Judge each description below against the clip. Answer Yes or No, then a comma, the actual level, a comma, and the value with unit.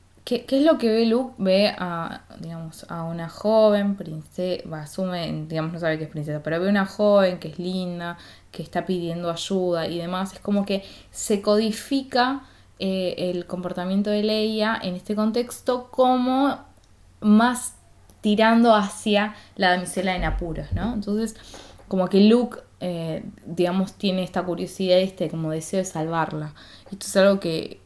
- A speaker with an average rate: Yes, average, 160 wpm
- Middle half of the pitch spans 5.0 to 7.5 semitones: No, average, 3.8 semitones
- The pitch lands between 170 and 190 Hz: Yes, medium, 185 Hz